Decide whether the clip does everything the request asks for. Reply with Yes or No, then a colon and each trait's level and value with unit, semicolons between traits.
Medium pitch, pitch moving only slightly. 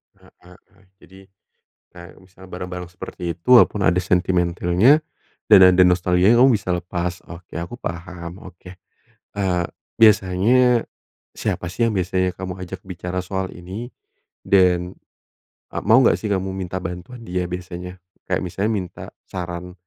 No: very low, 90 Hz; narrow, 1.6 semitones